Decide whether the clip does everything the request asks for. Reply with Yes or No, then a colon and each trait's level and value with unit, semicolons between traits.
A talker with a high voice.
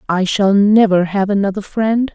Yes: high, 200 Hz